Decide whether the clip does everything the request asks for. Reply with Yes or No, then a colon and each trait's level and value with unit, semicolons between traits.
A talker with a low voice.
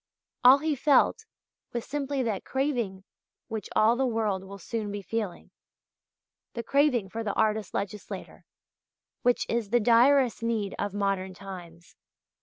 No: high, 225 Hz